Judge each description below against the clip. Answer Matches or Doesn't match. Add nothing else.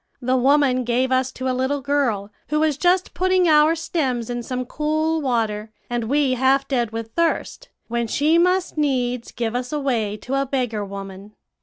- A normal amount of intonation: Matches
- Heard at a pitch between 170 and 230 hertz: Doesn't match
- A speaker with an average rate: Matches